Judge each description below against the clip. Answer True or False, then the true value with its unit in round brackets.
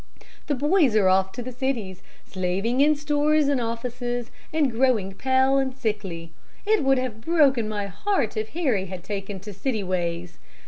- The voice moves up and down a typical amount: False (5.7 semitones)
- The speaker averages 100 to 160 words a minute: False (170 wpm)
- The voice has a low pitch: False (240 Hz)